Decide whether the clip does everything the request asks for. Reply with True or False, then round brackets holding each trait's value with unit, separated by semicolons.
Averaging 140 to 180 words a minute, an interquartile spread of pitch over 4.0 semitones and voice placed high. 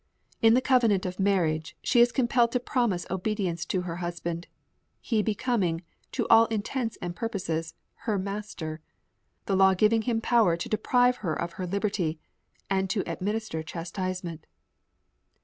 True (150 wpm; 4.6 semitones; 195 Hz)